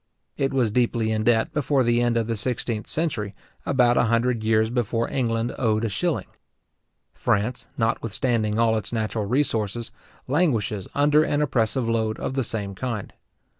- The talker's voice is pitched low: Yes, low, 115 Hz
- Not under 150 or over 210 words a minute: Yes, average, 160 wpm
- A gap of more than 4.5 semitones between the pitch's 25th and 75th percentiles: No, narrow, 2.6 semitones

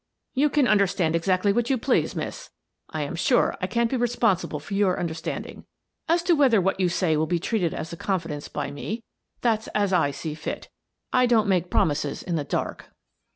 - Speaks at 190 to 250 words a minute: Yes, average, 200 wpm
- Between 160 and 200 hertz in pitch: Yes, high, 190 Hz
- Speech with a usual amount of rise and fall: No, wide, 6.1 semitones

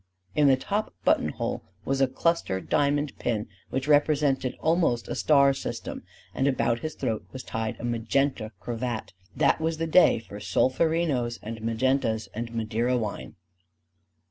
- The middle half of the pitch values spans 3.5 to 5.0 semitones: Yes, average, 4.3 semitones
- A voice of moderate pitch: No, low, 130 Hz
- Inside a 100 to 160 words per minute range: Yes, average, 150 wpm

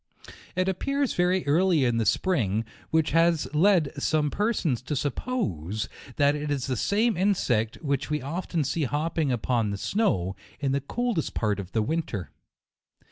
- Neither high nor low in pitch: Yes, medium, 150 Hz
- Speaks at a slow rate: No, average, 160 wpm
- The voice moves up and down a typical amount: No, wide, 6.9 semitones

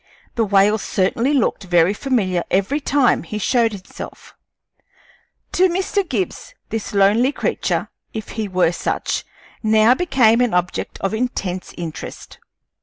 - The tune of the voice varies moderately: Yes, average, 4.8 semitones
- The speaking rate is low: Yes, slow, 130 wpm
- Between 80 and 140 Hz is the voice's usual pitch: No, high, 215 Hz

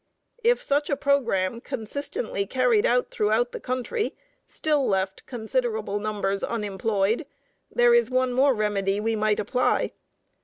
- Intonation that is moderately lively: Yes, average, 4.2 semitones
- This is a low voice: No, high, 230 Hz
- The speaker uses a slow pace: Yes, slow, 130 wpm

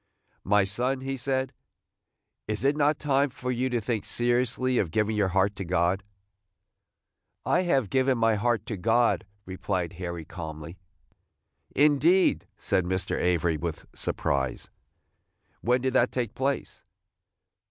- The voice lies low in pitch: Yes, low, 115 Hz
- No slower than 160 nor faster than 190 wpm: No, slow, 135 wpm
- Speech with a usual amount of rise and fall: No, wide, 5.9 semitones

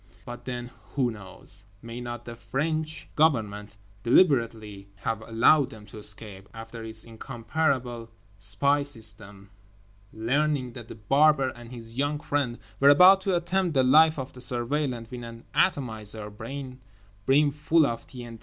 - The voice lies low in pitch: Yes, low, 120 Hz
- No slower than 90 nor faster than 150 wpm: Yes, slow, 135 wpm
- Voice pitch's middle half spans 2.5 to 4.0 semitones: No, average, 4.5 semitones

